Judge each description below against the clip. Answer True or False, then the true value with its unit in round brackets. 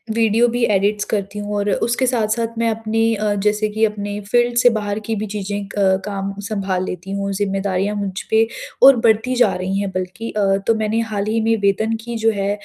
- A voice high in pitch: True (210 Hz)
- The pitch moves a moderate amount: False (2.2 semitones)